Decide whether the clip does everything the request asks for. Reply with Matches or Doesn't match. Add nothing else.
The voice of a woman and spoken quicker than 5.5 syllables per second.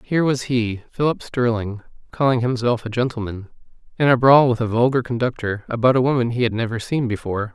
Doesn't match